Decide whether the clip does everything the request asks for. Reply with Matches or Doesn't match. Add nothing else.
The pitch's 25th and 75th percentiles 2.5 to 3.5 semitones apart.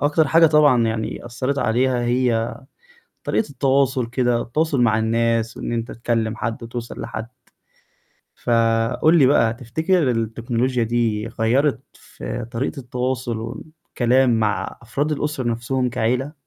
Matches